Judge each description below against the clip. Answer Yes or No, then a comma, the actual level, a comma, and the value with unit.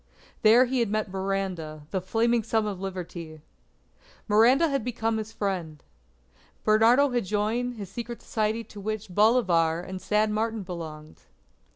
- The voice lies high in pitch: Yes, high, 210 Hz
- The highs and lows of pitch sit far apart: No, average, 3.6 semitones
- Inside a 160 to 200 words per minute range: No, average, 145 wpm